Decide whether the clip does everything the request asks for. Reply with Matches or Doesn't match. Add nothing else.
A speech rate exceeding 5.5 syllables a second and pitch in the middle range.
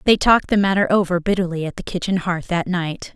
Matches